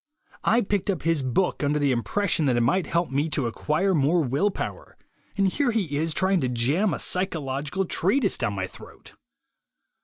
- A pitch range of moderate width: No, wide, 5.9 semitones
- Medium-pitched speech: Yes, medium, 160 Hz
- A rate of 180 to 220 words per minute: Yes, average, 185 wpm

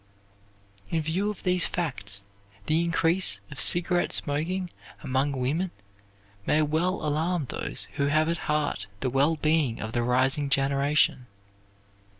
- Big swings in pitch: No, average, 3.8 semitones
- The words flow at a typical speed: No, slow, 130 wpm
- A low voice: No, medium, 150 Hz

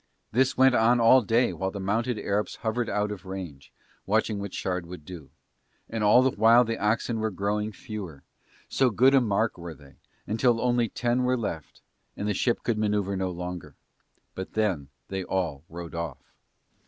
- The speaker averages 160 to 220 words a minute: Yes, average, 180 wpm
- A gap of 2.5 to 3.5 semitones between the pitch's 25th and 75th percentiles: No, average, 4.2 semitones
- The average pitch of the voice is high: No, low, 105 Hz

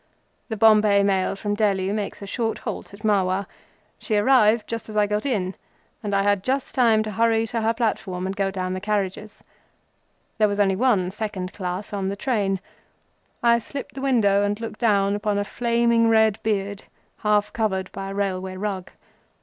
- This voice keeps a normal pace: Yes, average, 180 wpm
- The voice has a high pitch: Yes, high, 205 Hz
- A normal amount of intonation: No, narrow, 2.2 semitones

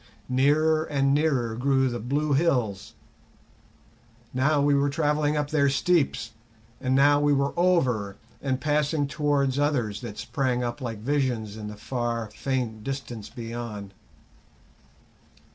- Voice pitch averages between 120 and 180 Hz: Yes, low, 135 Hz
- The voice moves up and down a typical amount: Yes, average, 3.7 semitones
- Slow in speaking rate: Yes, slow, 130 wpm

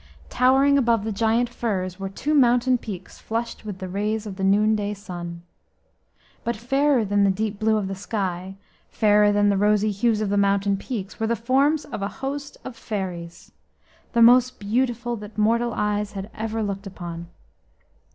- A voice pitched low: No, high, 210 Hz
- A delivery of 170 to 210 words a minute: Yes, average, 175 wpm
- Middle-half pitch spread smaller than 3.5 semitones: Yes, average, 3.1 semitones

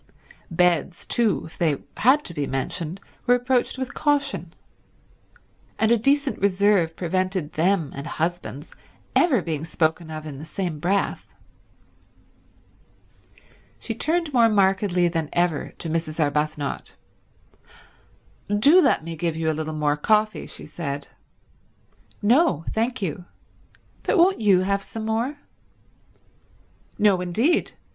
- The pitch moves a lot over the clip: Yes, wide, 5.9 semitones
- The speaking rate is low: Yes, slow, 125 wpm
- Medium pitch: Yes, medium, 180 Hz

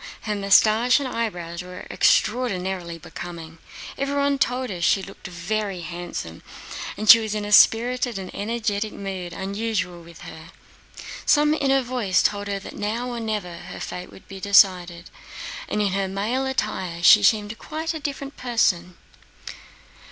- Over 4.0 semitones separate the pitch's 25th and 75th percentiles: Yes, average, 4.7 semitones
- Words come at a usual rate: Yes, average, 150 wpm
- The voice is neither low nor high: No, high, 205 Hz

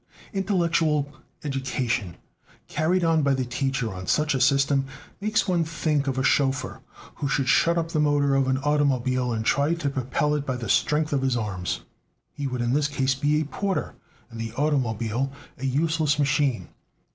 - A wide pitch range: No, average, 2.8 semitones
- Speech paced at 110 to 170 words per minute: No, average, 180 wpm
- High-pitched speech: No, medium, 140 Hz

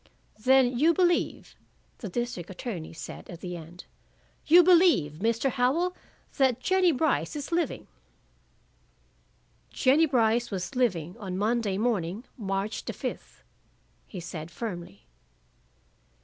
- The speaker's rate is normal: No, slow, 120 wpm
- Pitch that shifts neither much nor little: No, wide, 7.1 semitones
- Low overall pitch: No, high, 230 Hz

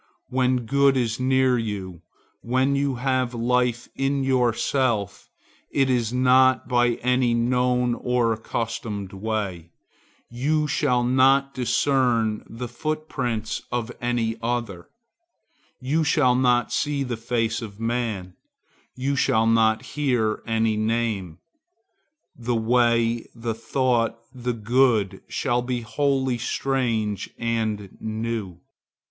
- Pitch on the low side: Yes, low, 120 Hz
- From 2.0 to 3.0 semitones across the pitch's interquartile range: Yes, narrow, 2.4 semitones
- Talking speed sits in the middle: No, slow, 110 wpm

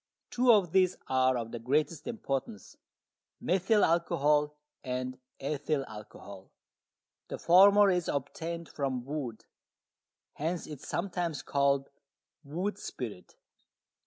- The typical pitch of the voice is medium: Yes, medium, 150 Hz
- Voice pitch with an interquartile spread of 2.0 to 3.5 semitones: No, average, 5.1 semitones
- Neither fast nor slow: No, slow, 110 wpm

